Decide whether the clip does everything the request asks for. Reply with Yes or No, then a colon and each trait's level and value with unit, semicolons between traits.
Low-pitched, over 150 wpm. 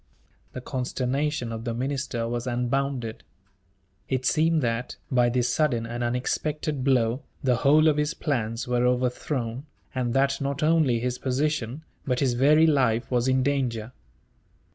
No: low, 130 Hz; average, 145 wpm